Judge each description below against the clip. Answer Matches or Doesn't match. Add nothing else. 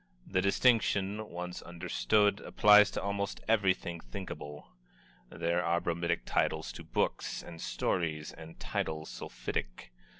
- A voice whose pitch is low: Matches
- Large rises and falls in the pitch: Doesn't match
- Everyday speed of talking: Doesn't match